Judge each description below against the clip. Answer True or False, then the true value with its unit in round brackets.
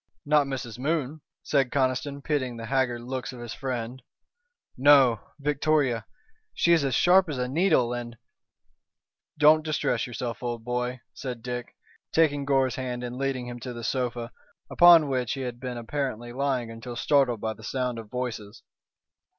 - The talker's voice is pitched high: False (125 Hz)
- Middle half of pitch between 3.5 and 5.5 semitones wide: False (2.8 semitones)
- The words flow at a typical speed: True (165 wpm)